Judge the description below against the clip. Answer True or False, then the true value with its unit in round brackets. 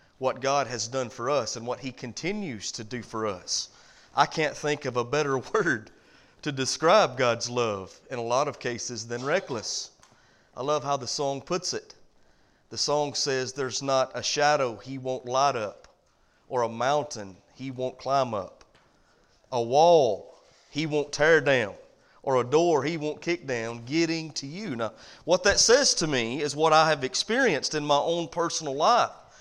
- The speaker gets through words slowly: False (180 wpm)